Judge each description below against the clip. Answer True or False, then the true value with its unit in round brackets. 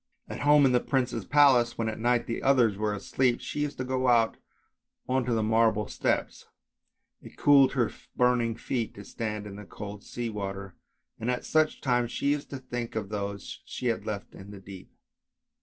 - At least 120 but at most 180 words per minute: False (195 wpm)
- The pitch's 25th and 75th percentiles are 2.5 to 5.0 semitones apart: True (3.5 semitones)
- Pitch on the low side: True (115 Hz)